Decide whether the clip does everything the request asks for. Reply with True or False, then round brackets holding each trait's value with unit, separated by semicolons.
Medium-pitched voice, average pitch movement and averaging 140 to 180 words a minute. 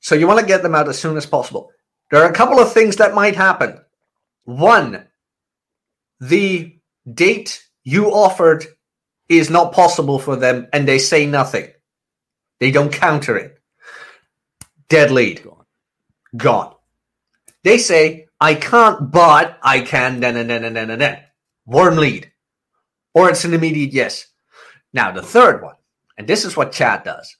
True (160 Hz; 4.5 semitones; 155 wpm)